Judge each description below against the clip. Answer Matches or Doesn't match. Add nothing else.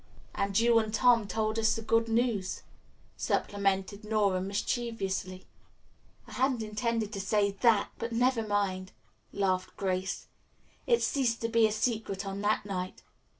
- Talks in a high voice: Matches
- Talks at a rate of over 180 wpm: Doesn't match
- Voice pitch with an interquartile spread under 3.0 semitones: Matches